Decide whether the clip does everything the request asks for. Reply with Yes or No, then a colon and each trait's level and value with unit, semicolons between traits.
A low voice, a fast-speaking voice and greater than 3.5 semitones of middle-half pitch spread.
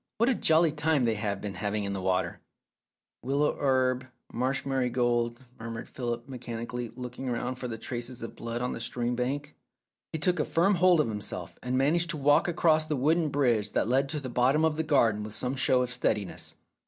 Yes: low, 125 Hz; fast, 210 wpm; average, 4.0 semitones